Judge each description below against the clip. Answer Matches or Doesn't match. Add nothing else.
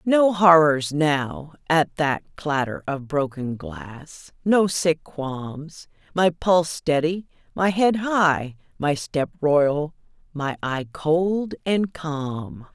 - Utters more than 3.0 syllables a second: Doesn't match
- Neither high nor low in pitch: Matches